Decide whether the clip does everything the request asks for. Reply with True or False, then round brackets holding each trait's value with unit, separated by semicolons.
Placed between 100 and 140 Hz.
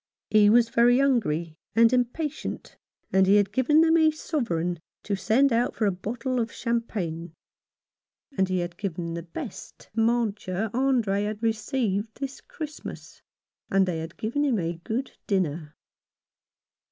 False (220 Hz)